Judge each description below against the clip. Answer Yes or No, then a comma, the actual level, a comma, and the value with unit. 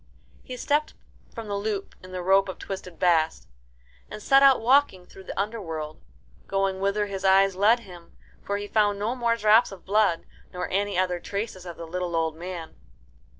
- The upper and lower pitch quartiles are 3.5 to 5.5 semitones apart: No, average, 2.9 semitones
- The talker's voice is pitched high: Yes, high, 195 Hz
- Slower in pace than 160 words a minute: No, average, 185 wpm